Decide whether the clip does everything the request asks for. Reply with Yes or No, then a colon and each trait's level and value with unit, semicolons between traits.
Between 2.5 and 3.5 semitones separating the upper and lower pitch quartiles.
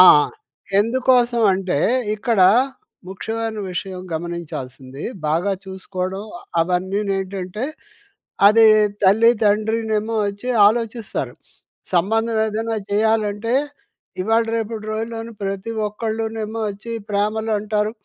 Yes: average, 2.8 semitones